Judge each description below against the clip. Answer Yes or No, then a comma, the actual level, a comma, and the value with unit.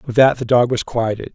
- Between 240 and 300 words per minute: Yes, fast, 270 wpm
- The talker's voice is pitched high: No, low, 120 Hz